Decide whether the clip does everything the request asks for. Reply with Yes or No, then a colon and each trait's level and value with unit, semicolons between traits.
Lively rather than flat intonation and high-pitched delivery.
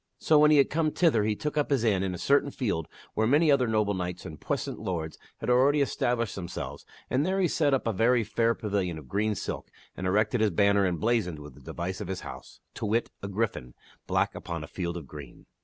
No: wide, 5.9 semitones; low, 105 Hz